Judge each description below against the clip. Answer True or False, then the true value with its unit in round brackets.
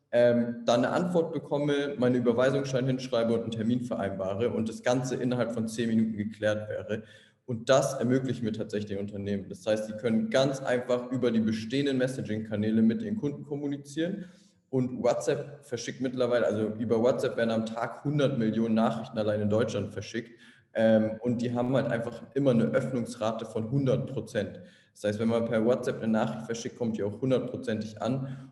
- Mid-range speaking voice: False (115 Hz)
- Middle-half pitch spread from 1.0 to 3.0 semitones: True (2.7 semitones)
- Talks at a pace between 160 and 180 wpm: True (175 wpm)